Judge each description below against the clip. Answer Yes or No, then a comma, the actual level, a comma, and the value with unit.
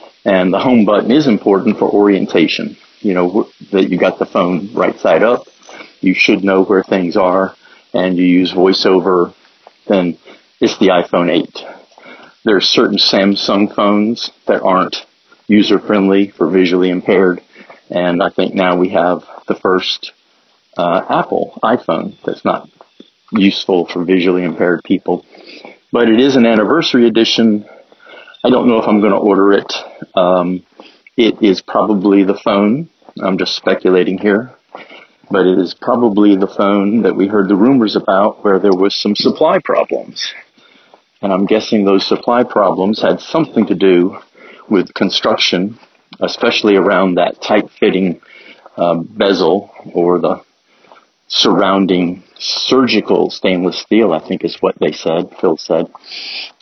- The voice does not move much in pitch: Yes, narrow, 2.2 semitones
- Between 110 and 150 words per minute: Yes, average, 145 wpm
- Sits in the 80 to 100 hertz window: Yes, very low, 95 Hz